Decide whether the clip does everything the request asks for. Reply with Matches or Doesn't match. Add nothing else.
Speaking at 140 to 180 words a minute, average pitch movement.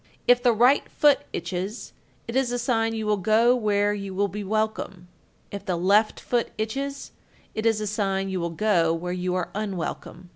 Doesn't match